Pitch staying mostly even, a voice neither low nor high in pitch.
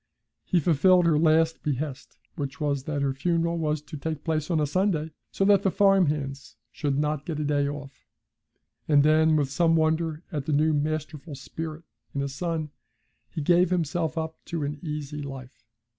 Yes: narrow, 2.3 semitones; medium, 155 Hz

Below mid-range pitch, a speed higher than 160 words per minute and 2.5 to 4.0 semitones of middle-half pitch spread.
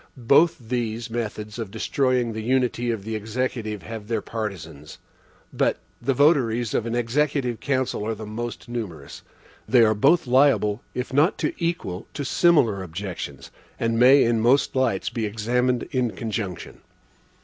No: low, 115 Hz; average, 155 wpm; average, 3.0 semitones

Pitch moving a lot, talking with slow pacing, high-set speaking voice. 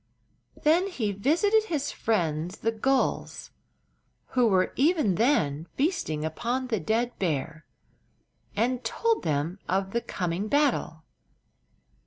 Yes: wide, 8.0 semitones; slow, 115 wpm; high, 225 Hz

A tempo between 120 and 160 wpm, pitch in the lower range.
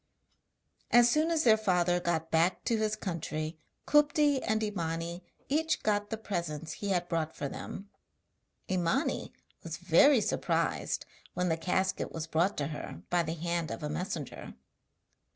No: average, 150 wpm; medium, 180 Hz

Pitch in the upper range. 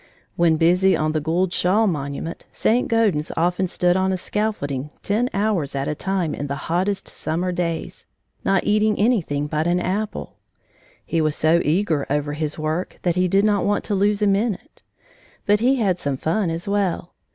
No: medium, 180 Hz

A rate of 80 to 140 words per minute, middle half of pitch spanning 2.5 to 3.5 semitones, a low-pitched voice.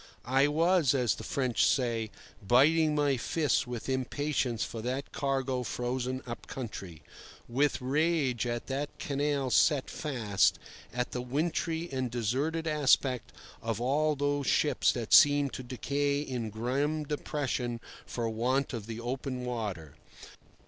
Yes: slow, 135 wpm; average, 3.1 semitones; low, 130 Hz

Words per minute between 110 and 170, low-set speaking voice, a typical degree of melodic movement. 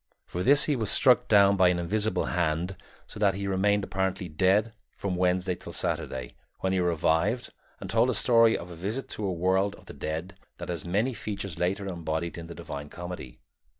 No: average, 200 wpm; very low, 95 Hz; average, 3.0 semitones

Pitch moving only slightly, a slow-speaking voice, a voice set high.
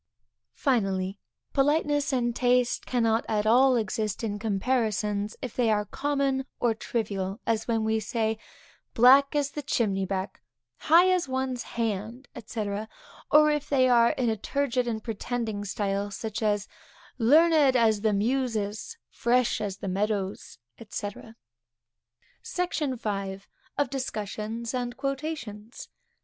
No: average, 4.0 semitones; slow, 130 wpm; high, 230 Hz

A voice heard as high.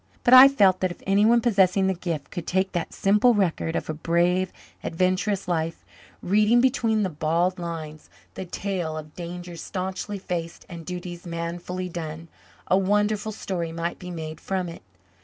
No: medium, 180 Hz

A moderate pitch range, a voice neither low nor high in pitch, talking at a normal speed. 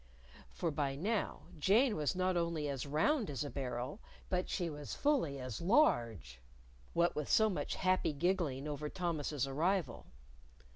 Yes: average, 5.0 semitones; medium, 155 Hz; average, 150 wpm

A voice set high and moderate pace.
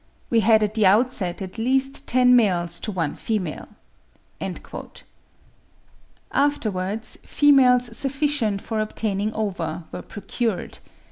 No: high, 220 Hz; slow, 110 wpm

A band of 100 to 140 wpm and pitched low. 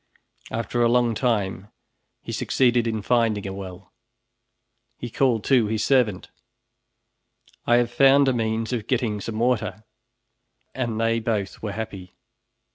Yes: slow, 135 wpm; low, 115 Hz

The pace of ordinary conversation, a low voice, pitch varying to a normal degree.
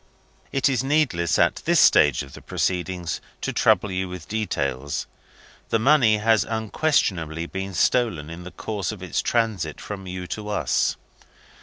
Yes: average, 155 wpm; very low, 95 Hz; average, 4.5 semitones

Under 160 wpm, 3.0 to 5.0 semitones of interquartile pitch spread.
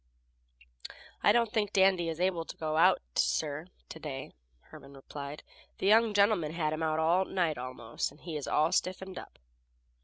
No: average, 175 wpm; average, 4.0 semitones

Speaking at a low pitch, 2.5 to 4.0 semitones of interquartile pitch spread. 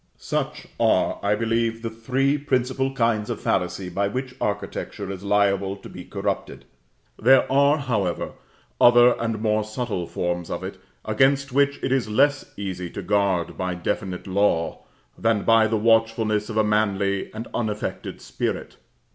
Yes: low, 110 Hz; average, 3.5 semitones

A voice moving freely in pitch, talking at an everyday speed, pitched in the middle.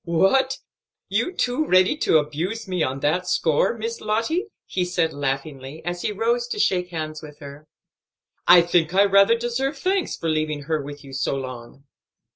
Yes: wide, 7.3 semitones; average, 175 wpm; medium, 175 Hz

